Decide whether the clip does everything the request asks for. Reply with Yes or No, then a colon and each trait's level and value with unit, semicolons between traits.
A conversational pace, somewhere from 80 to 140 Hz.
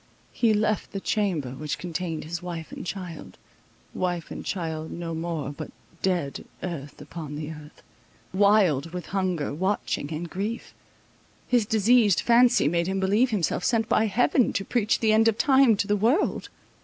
No: average, 155 wpm; medium, 185 Hz